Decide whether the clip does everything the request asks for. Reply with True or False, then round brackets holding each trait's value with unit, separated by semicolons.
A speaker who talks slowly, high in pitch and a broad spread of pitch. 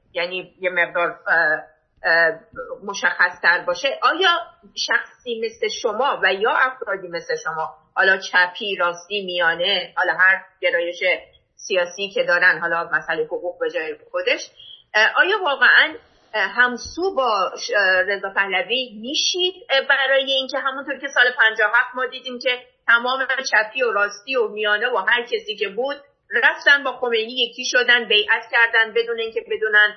False (135 wpm; 240 Hz; 7.0 semitones)